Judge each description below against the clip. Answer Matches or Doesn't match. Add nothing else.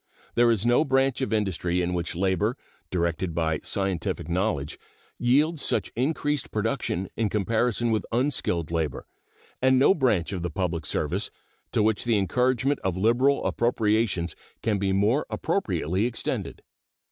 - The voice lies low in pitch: Matches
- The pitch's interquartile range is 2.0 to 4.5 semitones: Doesn't match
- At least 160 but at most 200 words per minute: Doesn't match